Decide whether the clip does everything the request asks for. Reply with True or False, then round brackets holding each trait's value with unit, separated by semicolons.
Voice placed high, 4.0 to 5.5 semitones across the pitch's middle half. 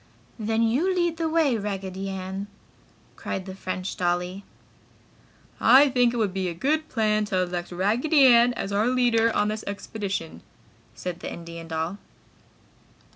True (205 Hz; 4.8 semitones)